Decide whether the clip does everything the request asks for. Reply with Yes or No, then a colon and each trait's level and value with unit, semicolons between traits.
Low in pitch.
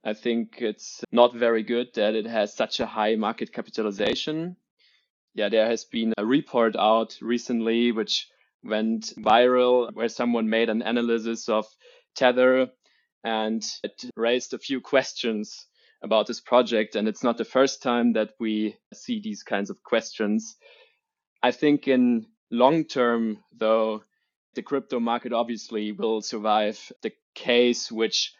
Yes: low, 120 Hz